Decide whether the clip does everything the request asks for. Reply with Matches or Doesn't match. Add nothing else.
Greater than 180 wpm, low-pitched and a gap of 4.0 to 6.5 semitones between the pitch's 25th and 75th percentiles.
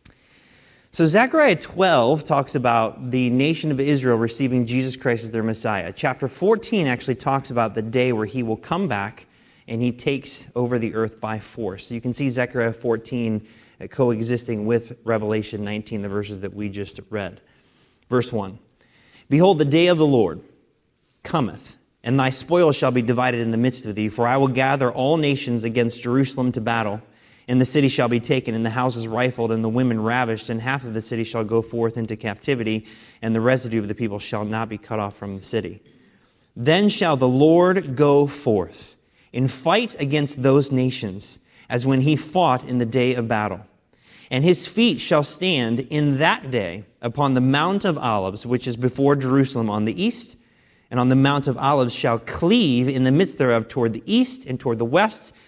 Doesn't match